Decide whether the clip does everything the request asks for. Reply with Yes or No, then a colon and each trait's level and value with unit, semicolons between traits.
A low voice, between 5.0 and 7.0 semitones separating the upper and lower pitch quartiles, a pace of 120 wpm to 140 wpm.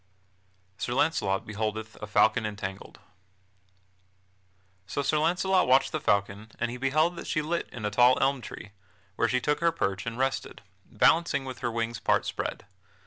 No: low, 120 Hz; wide, 5.5 semitones; average, 170 wpm